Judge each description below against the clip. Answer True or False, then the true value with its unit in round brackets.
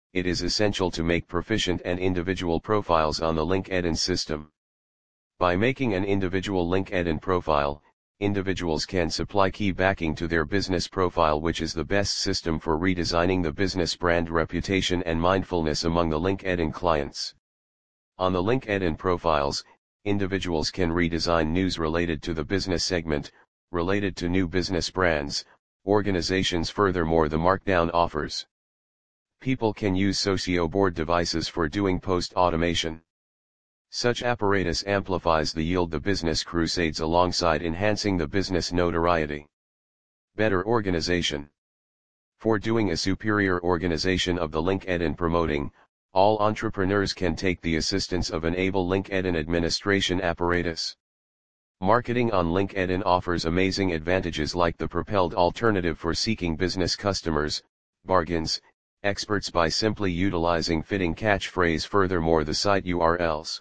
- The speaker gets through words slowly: True (130 wpm)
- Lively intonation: False (2.6 semitones)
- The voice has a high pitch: False (90 Hz)